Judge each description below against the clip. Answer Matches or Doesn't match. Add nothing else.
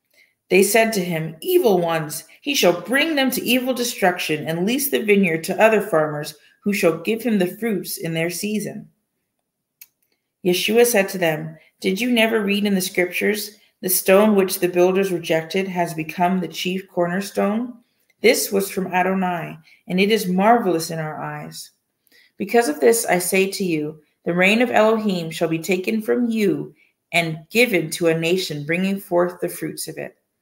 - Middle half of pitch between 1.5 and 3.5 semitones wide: Doesn't match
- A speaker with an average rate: Matches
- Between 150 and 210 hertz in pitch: Matches